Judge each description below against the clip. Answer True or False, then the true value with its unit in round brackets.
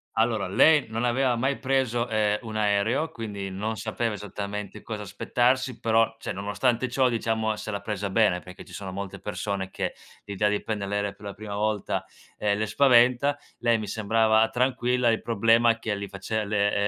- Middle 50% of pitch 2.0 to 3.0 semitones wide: True (2.6 semitones)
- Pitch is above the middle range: False (110 Hz)